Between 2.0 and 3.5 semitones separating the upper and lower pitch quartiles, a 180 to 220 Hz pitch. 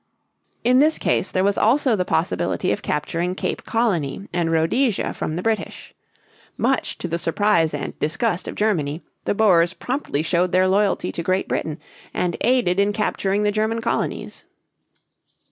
No: average, 4.5 semitones; high, 190 Hz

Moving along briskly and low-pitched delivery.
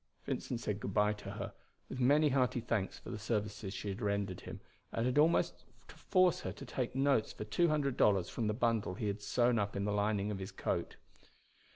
Yes: fast, 220 wpm; low, 110 Hz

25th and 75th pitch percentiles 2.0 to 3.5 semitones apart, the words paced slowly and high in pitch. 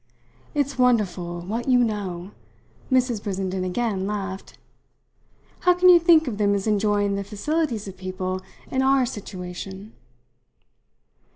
No: average, 4.8 semitones; slow, 125 wpm; high, 205 Hz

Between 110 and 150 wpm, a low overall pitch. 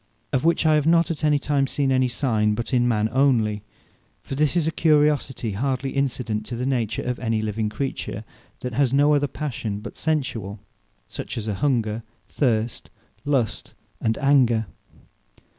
No: average, 170 wpm; low, 130 Hz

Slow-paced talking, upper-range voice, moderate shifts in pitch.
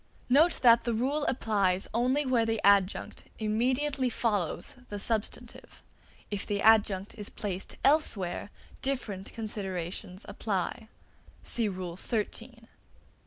Yes: slow, 120 wpm; high, 220 Hz; average, 3.9 semitones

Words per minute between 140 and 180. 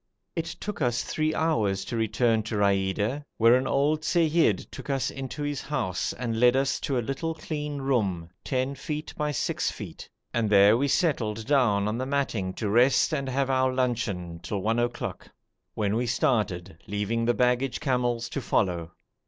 Yes: average, 175 wpm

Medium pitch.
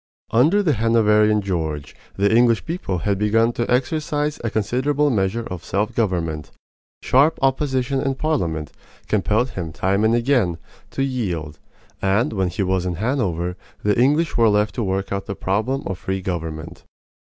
No: low, 105 Hz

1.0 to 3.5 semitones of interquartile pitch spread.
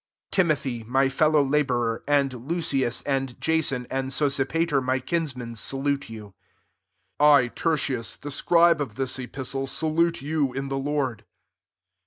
Yes: narrow, 2.6 semitones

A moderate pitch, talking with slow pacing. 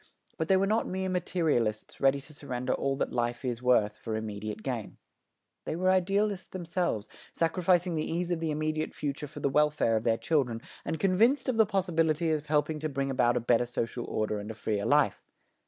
No: medium, 150 Hz; average, 200 wpm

